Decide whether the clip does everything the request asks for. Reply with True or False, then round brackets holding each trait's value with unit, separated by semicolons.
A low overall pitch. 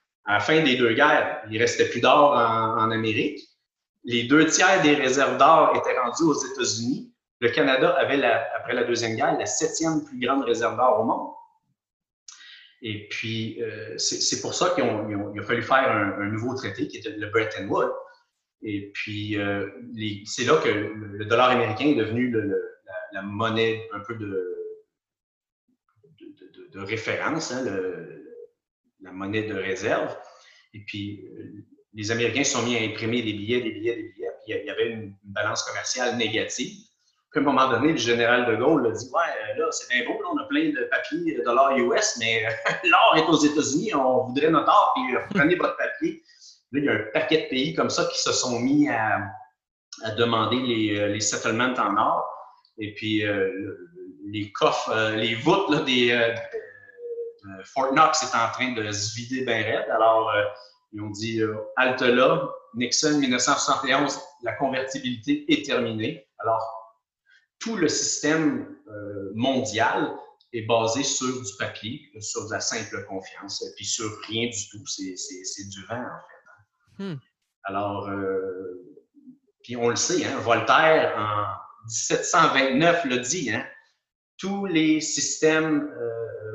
True (125 Hz)